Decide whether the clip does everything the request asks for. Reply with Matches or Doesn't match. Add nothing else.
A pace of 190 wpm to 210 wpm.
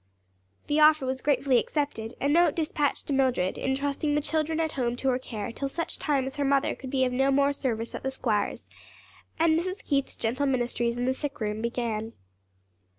Matches